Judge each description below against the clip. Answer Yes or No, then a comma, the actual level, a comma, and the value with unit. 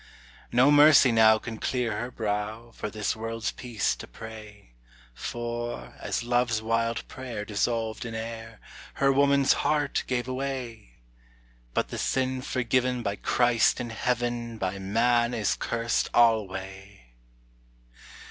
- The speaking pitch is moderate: No, low, 115 Hz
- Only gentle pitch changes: Yes, narrow, 2.1 semitones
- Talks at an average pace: No, slow, 130 wpm